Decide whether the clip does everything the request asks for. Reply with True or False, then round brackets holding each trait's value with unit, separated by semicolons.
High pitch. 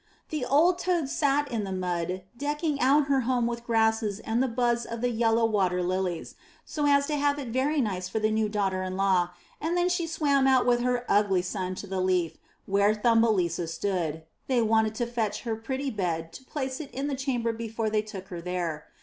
True (225 Hz)